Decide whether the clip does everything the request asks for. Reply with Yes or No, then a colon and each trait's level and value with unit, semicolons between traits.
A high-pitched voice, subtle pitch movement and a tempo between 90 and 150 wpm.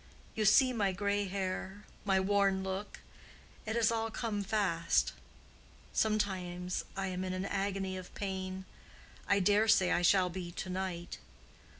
Yes: high, 195 Hz; narrow, 1.7 semitones; average, 140 wpm